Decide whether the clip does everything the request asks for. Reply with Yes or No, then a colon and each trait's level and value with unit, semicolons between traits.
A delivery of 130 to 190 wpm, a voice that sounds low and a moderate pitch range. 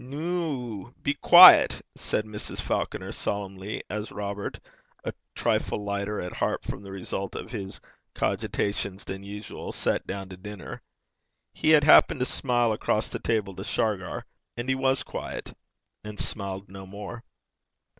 Yes: average, 145 wpm; low, 105 Hz; average, 3.6 semitones